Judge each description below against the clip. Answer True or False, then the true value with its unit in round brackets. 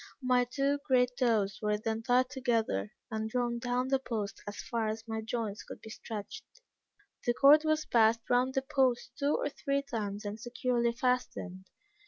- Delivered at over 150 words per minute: True (175 wpm)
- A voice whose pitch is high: True (240 Hz)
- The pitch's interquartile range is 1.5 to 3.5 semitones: True (2.8 semitones)